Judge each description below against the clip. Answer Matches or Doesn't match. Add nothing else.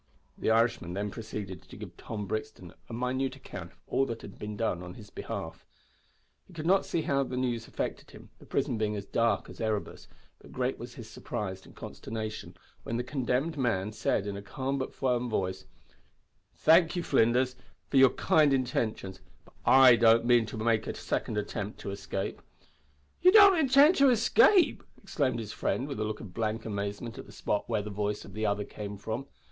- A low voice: Matches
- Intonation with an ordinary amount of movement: Matches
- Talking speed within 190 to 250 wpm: Matches